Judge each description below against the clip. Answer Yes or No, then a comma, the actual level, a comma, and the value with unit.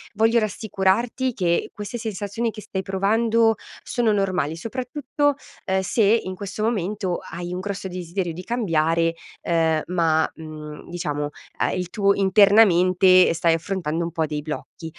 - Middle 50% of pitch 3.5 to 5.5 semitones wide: Yes, average, 4.3 semitones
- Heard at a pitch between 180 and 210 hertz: Yes, high, 190 Hz